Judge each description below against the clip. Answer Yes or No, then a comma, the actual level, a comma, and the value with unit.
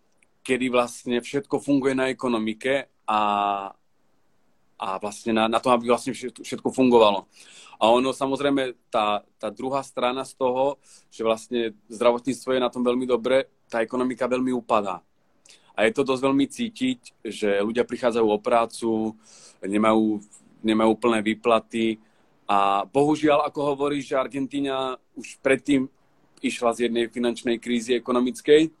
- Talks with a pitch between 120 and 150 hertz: Yes, low, 125 Hz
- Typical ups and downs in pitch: Yes, average, 3.0 semitones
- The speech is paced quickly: No, average, 135 wpm